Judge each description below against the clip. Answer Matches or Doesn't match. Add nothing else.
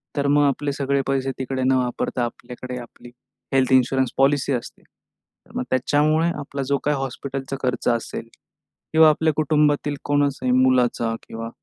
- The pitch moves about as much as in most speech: Doesn't match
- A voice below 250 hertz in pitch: Matches